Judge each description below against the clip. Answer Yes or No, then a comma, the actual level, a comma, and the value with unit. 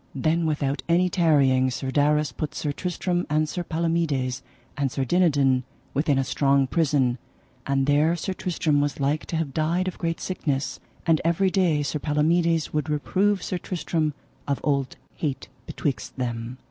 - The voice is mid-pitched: Yes, medium, 150 Hz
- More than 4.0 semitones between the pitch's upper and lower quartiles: No, average, 3.5 semitones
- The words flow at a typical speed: Yes, average, 160 wpm